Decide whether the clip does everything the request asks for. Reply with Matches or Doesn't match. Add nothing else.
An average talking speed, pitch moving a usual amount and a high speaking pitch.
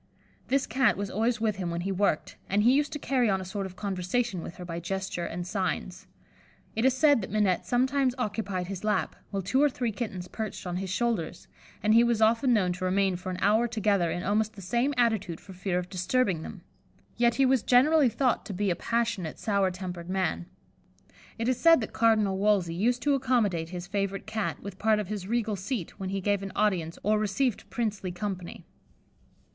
Doesn't match